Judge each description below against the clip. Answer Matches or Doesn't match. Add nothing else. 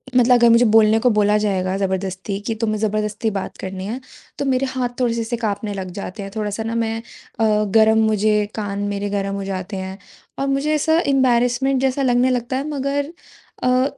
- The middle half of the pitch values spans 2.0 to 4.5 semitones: Matches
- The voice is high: Matches